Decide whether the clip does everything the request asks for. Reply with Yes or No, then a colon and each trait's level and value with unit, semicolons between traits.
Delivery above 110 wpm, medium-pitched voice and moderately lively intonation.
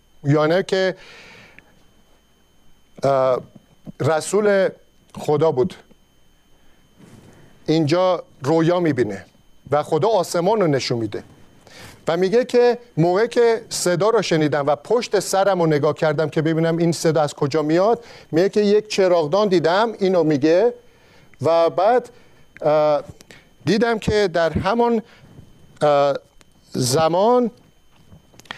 No: slow, 105 wpm; medium, 170 Hz; average, 4.9 semitones